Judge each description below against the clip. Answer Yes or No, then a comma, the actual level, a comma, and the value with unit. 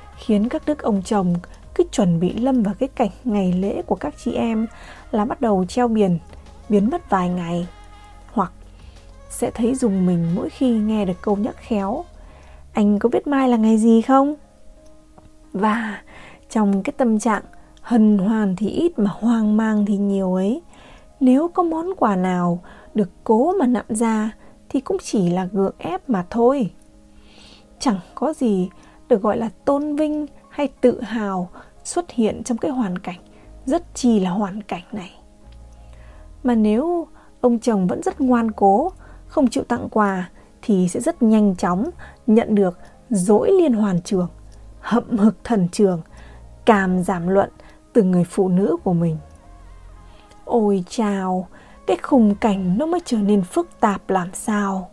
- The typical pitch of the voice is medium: No, high, 210 Hz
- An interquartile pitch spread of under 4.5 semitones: No, average, 4.8 semitones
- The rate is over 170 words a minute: No, slow, 165 wpm